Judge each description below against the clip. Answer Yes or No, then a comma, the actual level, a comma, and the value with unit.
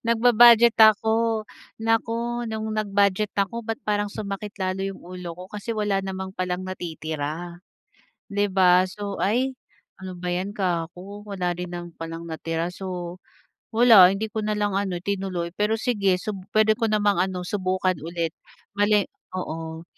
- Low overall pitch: No, high, 195 Hz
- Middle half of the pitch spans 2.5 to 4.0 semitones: Yes, average, 3.1 semitones